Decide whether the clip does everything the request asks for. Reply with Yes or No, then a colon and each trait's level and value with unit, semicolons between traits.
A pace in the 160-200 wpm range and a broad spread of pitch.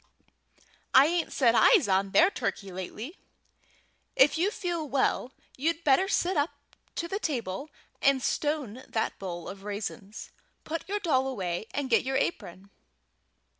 No: average, 145 wpm; wide, 8.1 semitones